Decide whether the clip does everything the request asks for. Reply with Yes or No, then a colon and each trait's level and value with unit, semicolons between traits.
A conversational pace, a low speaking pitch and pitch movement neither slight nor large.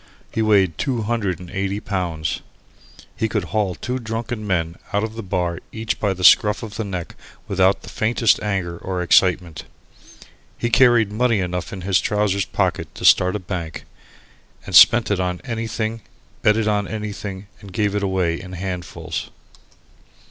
Yes: average, 170 wpm; low, 100 Hz; average, 3.1 semitones